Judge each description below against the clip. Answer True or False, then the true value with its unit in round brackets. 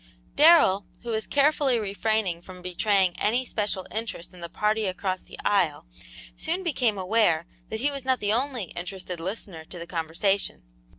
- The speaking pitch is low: False (205 Hz)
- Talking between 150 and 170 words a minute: True (165 wpm)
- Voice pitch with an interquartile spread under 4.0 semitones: False (4.3 semitones)